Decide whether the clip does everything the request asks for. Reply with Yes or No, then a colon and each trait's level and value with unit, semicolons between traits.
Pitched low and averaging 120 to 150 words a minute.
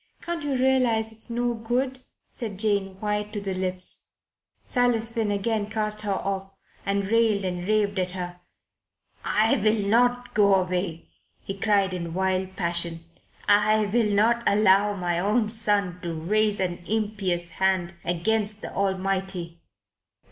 No: high, 205 Hz; average, 145 wpm